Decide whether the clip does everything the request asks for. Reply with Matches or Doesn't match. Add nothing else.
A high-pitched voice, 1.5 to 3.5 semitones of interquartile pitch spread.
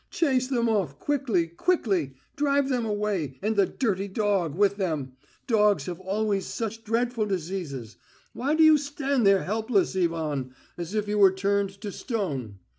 Doesn't match